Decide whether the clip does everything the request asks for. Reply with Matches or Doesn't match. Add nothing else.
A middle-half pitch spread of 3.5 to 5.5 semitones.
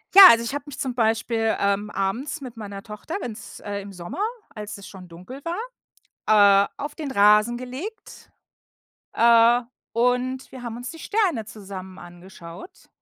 Matches